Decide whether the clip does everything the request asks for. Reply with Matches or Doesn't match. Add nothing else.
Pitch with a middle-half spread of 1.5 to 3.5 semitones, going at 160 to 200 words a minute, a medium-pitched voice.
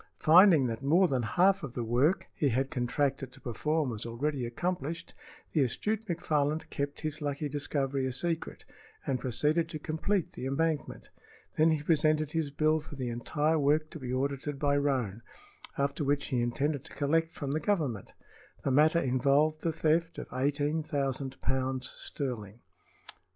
Matches